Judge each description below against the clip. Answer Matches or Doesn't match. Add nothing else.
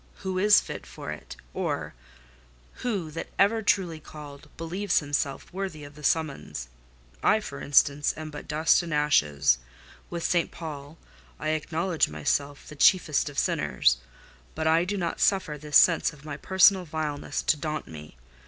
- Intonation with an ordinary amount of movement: Matches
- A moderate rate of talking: Matches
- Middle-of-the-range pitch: Matches